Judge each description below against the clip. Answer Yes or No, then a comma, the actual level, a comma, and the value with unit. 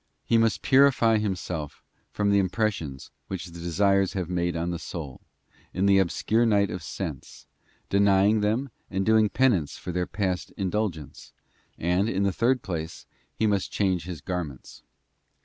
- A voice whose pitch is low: Yes, very low, 95 Hz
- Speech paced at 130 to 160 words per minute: Yes, average, 155 wpm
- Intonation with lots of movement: No, average, 3.4 semitones